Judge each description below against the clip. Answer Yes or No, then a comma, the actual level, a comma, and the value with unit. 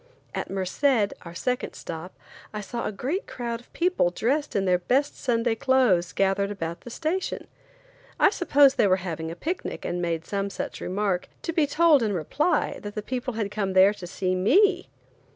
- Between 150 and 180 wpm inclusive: No, average, 190 wpm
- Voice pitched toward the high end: Yes, high, 210 Hz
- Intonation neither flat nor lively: No, wide, 6.6 semitones